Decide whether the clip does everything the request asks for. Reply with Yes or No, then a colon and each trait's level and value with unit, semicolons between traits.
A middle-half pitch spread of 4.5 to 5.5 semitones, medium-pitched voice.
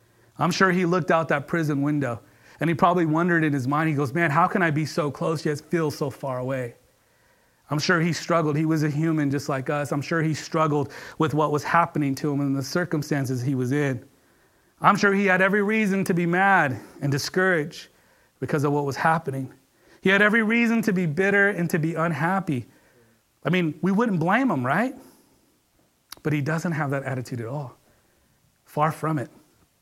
No: average, 3.8 semitones; medium, 155 Hz